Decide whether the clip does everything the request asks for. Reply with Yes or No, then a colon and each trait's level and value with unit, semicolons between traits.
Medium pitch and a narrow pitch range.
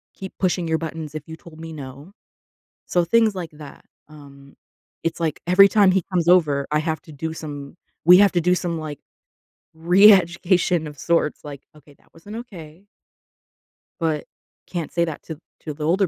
No: medium, 165 Hz; average, 3.0 semitones